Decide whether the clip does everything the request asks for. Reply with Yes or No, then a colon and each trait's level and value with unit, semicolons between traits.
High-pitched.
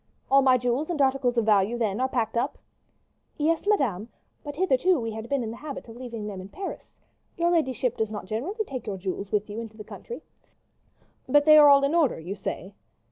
Yes: high, 245 Hz